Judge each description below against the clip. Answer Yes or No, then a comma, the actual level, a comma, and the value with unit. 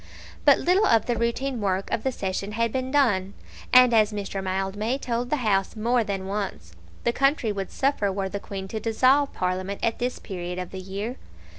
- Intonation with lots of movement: No, average, 4.3 semitones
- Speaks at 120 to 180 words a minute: No, average, 195 wpm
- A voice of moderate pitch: No, high, 215 Hz